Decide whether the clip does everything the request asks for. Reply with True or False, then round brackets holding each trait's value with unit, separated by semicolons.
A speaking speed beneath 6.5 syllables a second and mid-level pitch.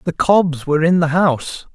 True (5.1 syllables/s; 160 Hz)